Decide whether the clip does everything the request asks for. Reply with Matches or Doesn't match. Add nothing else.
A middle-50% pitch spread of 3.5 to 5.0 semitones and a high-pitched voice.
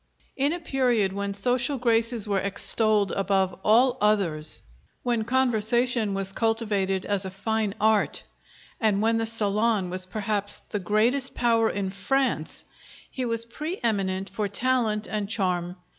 Doesn't match